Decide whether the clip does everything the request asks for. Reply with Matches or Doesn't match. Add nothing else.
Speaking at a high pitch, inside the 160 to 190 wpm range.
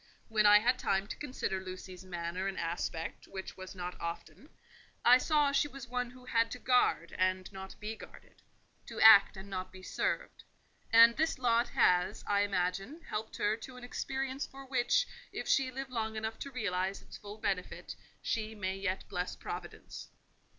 Matches